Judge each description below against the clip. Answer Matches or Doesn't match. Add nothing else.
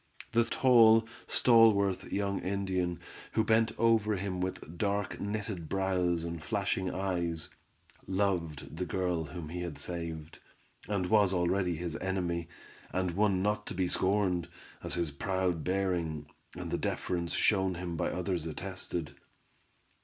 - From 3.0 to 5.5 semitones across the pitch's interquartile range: Doesn't match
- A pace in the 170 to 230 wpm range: Doesn't match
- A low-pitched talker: Matches